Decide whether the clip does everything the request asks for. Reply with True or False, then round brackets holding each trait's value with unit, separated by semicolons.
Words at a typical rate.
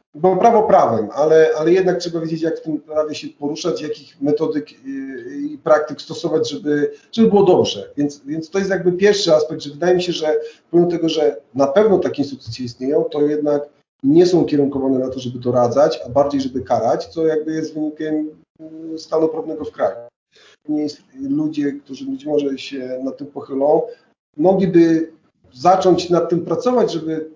False (170 wpm)